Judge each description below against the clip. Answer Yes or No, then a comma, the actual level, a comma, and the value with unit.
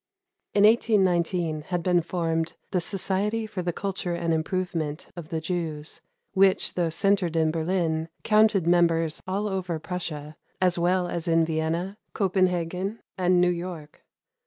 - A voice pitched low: No, medium, 175 Hz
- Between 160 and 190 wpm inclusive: No, average, 140 wpm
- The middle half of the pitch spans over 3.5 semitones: No, narrow, 2.4 semitones